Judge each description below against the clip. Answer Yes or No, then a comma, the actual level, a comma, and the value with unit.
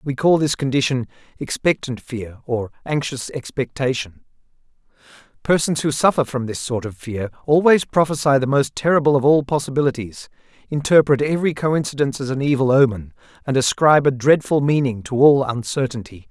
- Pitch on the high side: No, low, 135 Hz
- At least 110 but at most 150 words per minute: Yes, average, 145 wpm